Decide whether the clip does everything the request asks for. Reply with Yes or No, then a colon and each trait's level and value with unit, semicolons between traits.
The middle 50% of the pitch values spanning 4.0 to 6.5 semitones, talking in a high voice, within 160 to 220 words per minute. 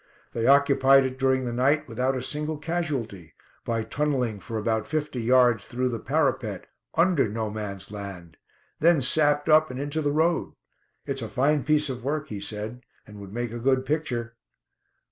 No: average, 4.5 semitones; low, 130 Hz; average, 175 wpm